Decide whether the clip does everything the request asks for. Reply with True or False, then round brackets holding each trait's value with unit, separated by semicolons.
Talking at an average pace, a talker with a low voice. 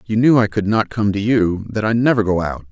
False (265 wpm; 105 Hz)